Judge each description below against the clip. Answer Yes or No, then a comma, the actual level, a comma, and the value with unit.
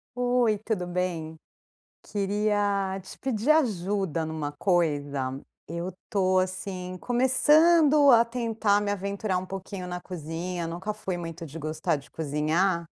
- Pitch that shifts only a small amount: No, average, 4.1 semitones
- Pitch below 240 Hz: Yes, medium, 185 Hz